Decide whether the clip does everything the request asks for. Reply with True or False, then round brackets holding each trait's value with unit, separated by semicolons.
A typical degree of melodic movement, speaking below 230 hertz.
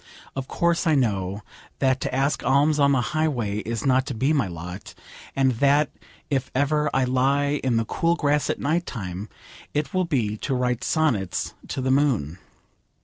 True (4.2 semitones; 135 Hz)